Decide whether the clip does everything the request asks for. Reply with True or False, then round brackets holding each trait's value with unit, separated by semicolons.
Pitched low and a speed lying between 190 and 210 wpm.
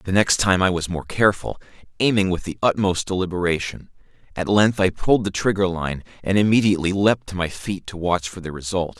True (95 Hz; 200 wpm)